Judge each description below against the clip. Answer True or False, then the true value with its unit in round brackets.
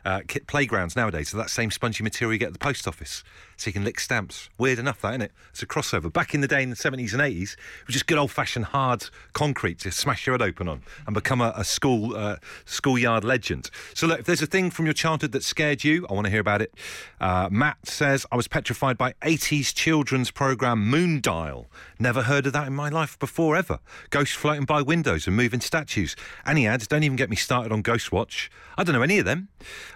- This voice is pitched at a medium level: False (125 Hz)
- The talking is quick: True (240 wpm)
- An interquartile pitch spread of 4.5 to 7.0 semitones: True (5.3 semitones)